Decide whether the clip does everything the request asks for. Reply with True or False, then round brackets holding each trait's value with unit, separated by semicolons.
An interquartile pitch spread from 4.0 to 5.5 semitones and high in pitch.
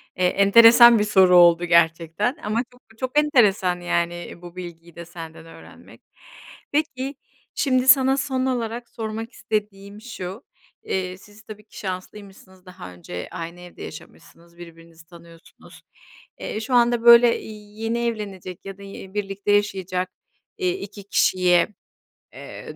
True (4.7 semitones; 200 Hz)